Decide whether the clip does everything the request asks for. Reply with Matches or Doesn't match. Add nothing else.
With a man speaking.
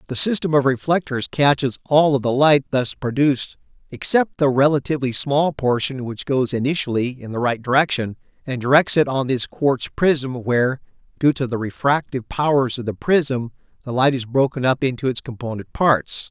Matches